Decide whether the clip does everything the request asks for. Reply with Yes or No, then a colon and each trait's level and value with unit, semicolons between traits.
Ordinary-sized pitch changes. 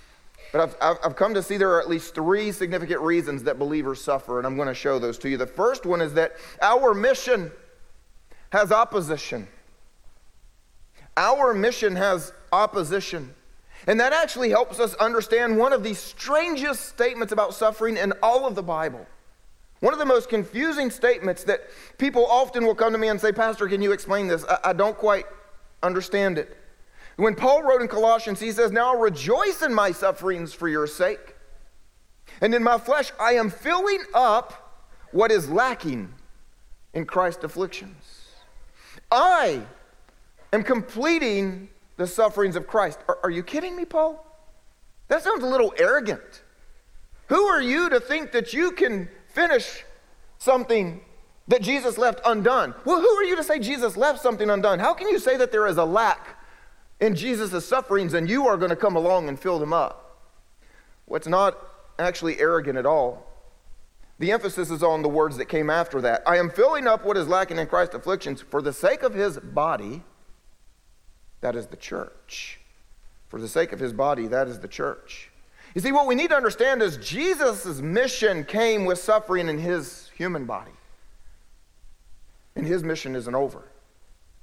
No: wide, 6.5 semitones